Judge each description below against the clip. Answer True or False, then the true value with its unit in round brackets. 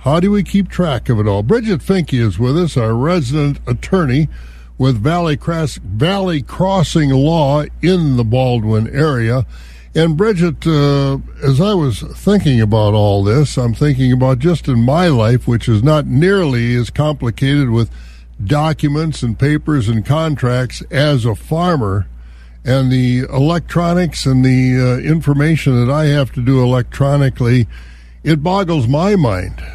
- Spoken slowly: False (150 wpm)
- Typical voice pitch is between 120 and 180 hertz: True (135 Hz)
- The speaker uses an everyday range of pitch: True (4.8 semitones)